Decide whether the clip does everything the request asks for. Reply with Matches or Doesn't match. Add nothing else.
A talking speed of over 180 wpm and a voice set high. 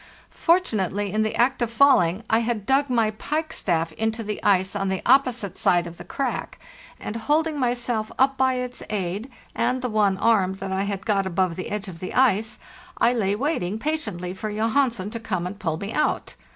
Matches